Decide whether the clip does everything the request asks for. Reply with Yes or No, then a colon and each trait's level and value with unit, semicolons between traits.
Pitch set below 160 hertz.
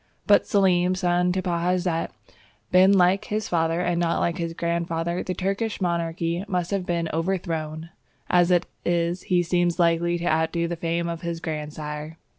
No: medium, 170 Hz